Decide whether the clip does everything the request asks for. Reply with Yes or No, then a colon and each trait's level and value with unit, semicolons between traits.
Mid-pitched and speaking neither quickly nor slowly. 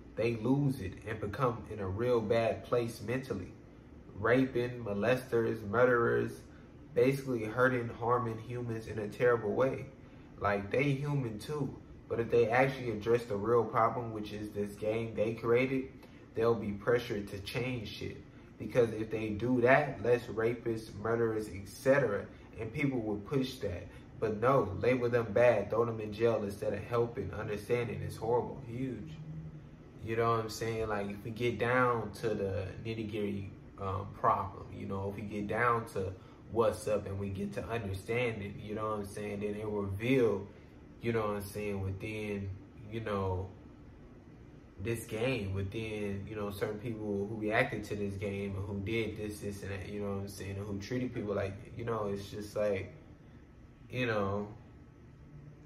No: low, 110 Hz; average, 170 wpm